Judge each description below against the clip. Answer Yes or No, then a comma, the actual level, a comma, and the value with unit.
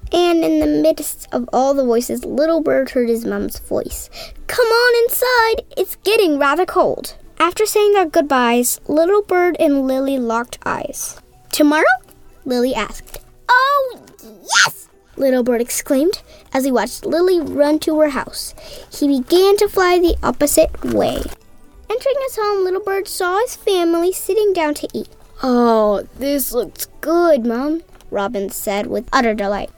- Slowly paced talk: No, average, 155 wpm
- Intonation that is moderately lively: No, wide, 6.4 semitones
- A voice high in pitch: Yes, very high, 315 Hz